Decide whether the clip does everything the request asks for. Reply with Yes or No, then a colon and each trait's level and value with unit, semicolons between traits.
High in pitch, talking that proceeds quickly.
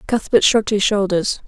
No: high, 210 Hz; average, 165 wpm